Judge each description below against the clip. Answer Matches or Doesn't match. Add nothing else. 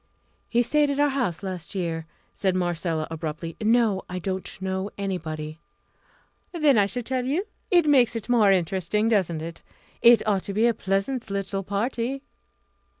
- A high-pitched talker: Matches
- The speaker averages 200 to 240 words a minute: Doesn't match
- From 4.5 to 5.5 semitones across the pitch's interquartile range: Matches